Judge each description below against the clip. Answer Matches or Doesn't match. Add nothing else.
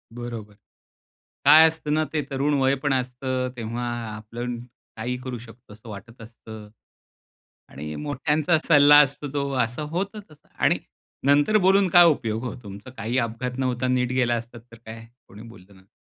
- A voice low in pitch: Matches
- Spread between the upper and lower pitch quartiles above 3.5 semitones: Matches